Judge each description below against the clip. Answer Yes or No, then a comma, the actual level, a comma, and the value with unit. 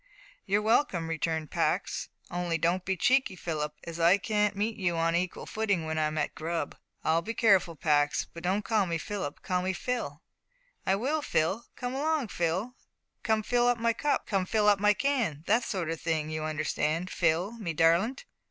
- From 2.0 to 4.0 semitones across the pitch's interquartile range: No, average, 5.0 semitones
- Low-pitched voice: No, medium, 185 Hz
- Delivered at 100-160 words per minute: No, average, 190 wpm